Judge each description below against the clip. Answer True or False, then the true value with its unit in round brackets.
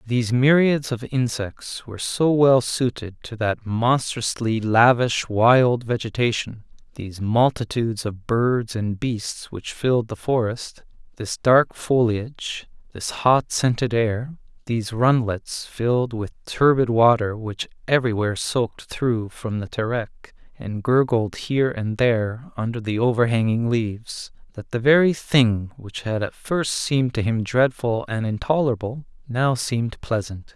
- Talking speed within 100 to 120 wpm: False (135 wpm)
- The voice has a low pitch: True (120 Hz)